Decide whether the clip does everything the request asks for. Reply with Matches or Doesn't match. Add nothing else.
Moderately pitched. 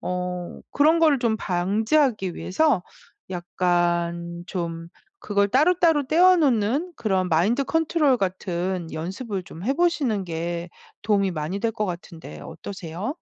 Doesn't match